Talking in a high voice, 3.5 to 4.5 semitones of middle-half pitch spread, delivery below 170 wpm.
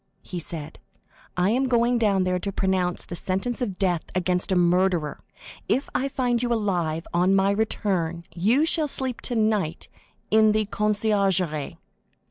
Yes: high, 195 Hz; average, 4.0 semitones; average, 150 wpm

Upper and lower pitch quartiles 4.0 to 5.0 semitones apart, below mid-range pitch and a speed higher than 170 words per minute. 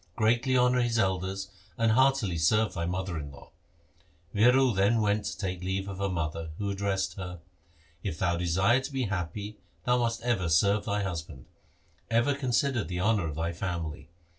Yes: average, 4.7 semitones; low, 100 Hz; average, 180 wpm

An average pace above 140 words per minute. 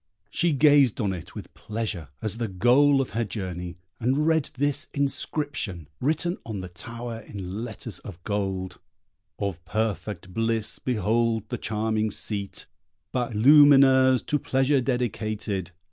No: slow, 135 wpm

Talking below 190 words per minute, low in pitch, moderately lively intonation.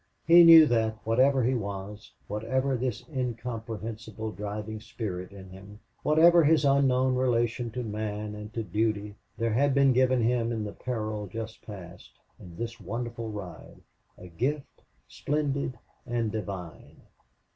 Yes: average, 140 wpm; low, 115 Hz; average, 3.5 semitones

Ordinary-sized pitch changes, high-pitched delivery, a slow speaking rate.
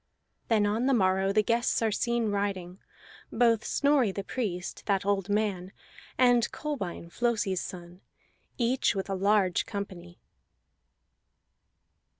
Yes: average, 3.7 semitones; high, 205 Hz; slow, 125 wpm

